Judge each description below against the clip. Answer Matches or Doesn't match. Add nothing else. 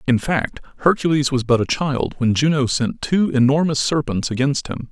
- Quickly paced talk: Doesn't match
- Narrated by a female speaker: Doesn't match